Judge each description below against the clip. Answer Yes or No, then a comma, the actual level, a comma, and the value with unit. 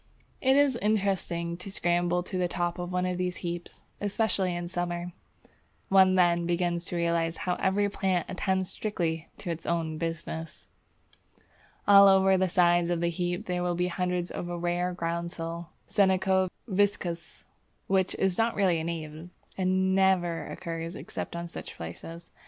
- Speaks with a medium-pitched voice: Yes, medium, 175 Hz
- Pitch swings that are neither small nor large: No, narrow, 1.7 semitones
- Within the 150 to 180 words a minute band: Yes, average, 160 wpm